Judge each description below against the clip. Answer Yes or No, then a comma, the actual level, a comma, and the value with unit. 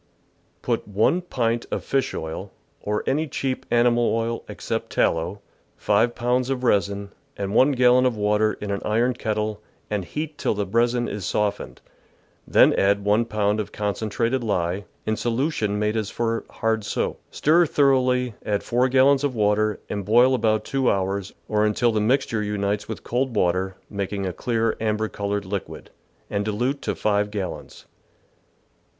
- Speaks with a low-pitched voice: Yes, low, 110 Hz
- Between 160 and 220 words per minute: Yes, average, 165 wpm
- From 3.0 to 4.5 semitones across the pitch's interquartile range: Yes, average, 3.3 semitones